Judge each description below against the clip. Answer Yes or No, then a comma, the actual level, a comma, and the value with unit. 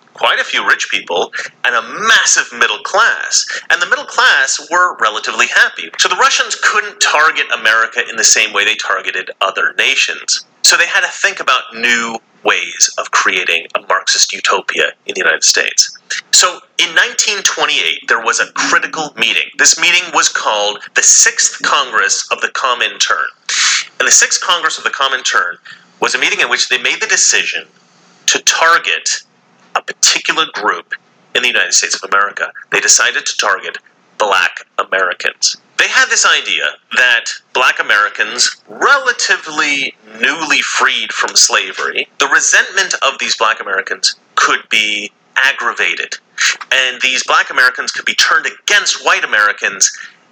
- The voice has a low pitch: Yes, low, 120 Hz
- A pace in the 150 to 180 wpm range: Yes, average, 155 wpm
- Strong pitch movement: Yes, wide, 8.7 semitones